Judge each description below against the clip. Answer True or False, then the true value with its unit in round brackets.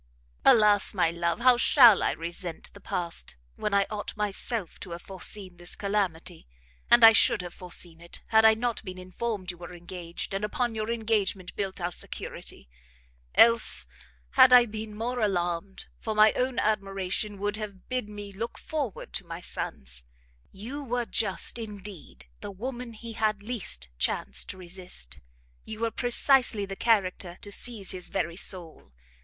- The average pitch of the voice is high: True (200 Hz)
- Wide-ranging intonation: False (3.9 semitones)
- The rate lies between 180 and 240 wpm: False (165 wpm)